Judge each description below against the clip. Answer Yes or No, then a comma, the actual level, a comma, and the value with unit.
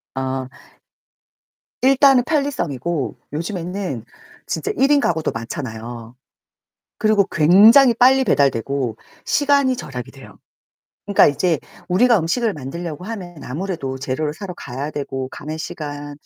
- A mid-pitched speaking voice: Yes, medium, 165 Hz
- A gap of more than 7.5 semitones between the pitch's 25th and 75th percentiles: Yes, wide, 8.1 semitones